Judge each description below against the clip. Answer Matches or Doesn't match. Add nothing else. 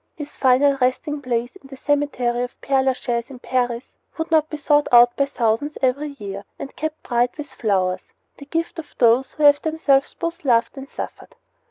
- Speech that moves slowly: Doesn't match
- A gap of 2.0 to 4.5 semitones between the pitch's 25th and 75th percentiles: Matches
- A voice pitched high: Matches